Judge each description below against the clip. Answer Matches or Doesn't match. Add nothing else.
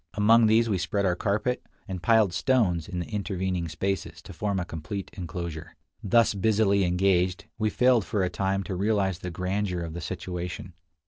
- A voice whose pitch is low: Matches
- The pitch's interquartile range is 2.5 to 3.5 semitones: Matches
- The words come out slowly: Doesn't match